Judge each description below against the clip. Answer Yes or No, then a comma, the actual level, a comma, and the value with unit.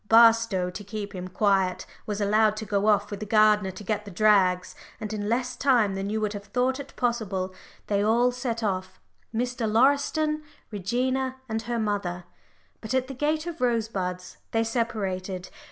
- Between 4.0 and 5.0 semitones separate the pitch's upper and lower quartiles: No, average, 3.4 semitones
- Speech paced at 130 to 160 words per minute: No, average, 175 wpm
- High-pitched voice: Yes, high, 215 Hz